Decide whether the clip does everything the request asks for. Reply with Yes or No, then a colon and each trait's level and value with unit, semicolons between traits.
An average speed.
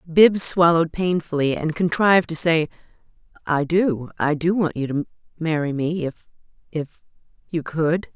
No: slow, 120 wpm